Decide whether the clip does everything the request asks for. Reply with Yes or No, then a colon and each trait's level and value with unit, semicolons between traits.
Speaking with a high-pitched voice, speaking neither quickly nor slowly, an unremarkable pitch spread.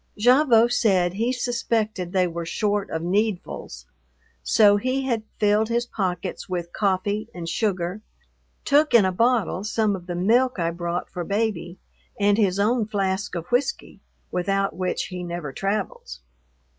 Yes: high, 200 Hz; average, 150 wpm; average, 4.0 semitones